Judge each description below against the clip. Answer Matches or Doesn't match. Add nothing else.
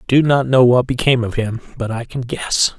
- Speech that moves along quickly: Matches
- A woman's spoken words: Doesn't match